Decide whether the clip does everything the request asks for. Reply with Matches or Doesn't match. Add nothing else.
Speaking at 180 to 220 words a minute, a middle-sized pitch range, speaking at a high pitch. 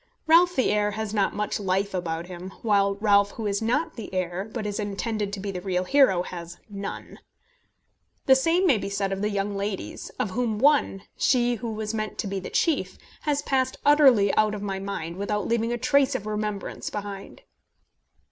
Matches